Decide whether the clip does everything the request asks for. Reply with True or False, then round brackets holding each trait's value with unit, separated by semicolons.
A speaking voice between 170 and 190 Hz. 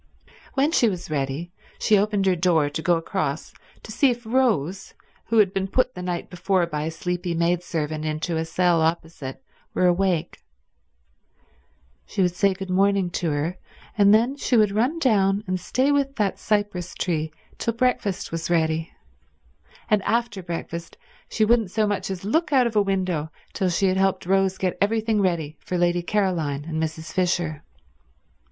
True (185 Hz)